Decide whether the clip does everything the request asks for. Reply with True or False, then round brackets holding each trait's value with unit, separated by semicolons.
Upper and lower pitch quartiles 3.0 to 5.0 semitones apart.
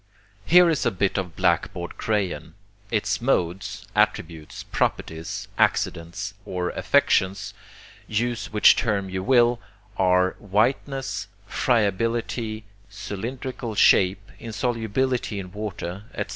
True (4.0 semitones)